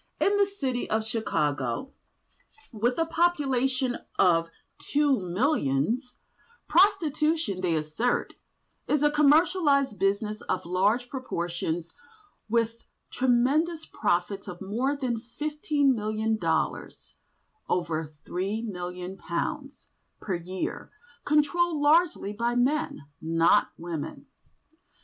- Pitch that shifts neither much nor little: No, wide, 8.2 semitones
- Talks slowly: Yes, slow, 95 wpm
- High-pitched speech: Yes, high, 235 Hz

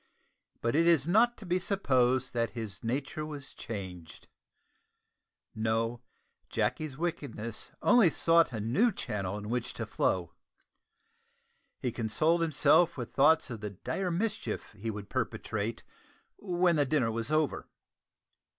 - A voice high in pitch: No, low, 130 Hz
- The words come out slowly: Yes, slow, 130 wpm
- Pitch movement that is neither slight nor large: No, wide, 6.9 semitones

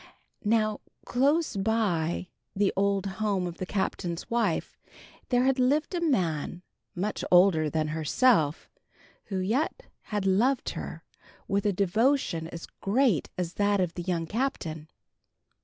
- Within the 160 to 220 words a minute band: No, slow, 135 wpm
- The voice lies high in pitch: Yes, high, 195 Hz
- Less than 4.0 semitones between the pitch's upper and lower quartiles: No, average, 5.1 semitones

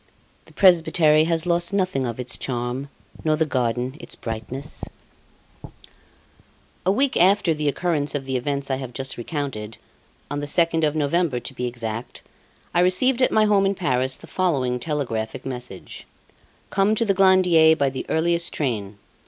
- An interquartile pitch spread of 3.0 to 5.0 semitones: No, wide, 5.5 semitones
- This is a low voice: No, medium, 150 Hz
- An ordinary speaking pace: Yes, average, 160 wpm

